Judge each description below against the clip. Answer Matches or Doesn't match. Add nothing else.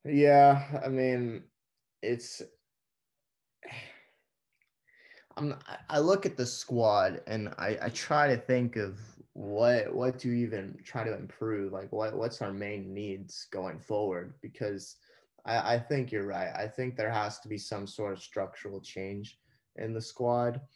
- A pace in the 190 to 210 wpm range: Doesn't match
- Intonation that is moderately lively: Matches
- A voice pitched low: Matches